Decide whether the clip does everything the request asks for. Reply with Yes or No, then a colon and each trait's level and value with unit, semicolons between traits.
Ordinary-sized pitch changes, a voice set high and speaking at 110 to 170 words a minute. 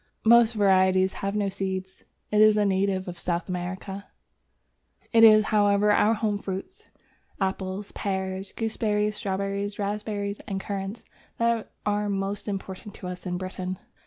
No: narrow, 1.7 semitones; high, 200 Hz; average, 140 wpm